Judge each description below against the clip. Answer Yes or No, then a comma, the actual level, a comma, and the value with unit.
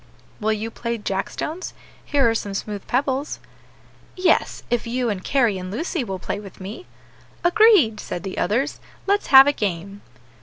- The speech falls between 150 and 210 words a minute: Yes, average, 165 wpm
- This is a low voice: No, high, 230 Hz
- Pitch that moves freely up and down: Yes, wide, 5.9 semitones